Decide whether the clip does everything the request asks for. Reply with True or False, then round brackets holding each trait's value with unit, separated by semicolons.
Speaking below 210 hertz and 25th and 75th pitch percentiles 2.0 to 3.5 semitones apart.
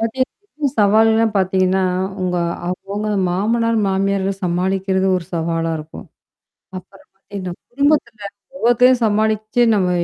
True (195 Hz; 3.2 semitones)